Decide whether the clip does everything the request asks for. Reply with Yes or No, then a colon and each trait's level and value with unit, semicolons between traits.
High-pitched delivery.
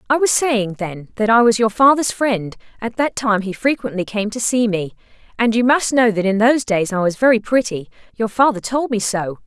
Yes: high, 225 Hz